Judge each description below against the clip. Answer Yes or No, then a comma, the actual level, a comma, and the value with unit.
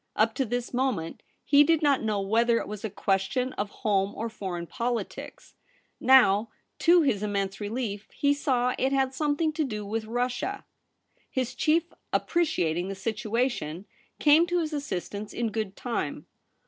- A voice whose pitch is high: Yes, high, 235 Hz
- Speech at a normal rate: Yes, average, 160 wpm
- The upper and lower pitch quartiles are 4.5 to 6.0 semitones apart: Yes, average, 4.9 semitones